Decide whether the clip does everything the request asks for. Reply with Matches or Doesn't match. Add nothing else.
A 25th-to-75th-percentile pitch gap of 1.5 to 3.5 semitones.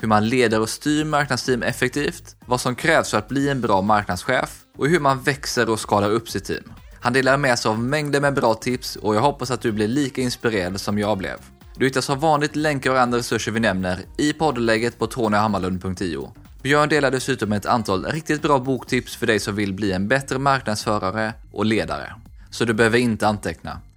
Doesn't match